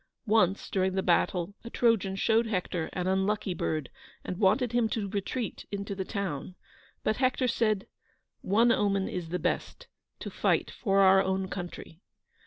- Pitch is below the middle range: No, high, 195 Hz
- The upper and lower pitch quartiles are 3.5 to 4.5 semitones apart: No, average, 2.8 semitones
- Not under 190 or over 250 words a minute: No, average, 160 wpm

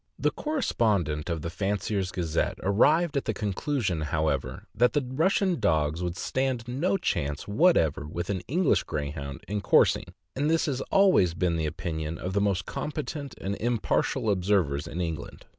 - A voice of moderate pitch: No, low, 100 Hz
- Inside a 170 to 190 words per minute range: Yes, average, 175 wpm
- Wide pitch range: Yes, wide, 8.3 semitones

